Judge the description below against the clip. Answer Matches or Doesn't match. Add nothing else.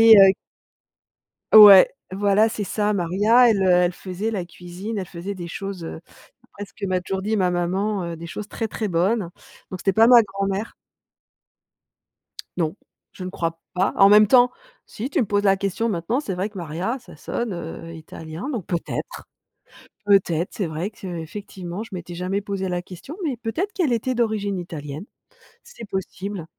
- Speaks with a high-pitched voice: Matches